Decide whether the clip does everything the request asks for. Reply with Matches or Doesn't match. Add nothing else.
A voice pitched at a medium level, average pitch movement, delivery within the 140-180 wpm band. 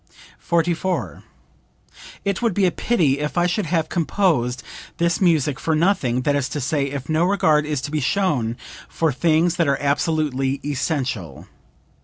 Matches